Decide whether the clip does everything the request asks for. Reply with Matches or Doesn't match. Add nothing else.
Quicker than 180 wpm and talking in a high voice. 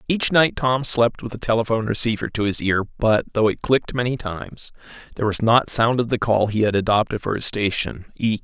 Doesn't match